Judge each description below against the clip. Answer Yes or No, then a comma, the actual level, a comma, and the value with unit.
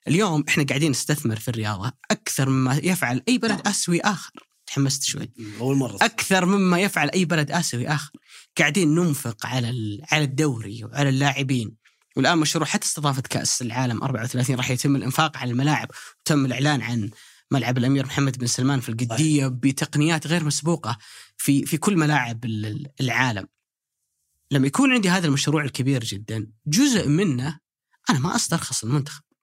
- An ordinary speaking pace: No, fast, 150 wpm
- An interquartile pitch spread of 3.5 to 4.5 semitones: Yes, average, 4.0 semitones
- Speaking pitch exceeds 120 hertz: Yes, medium, 140 Hz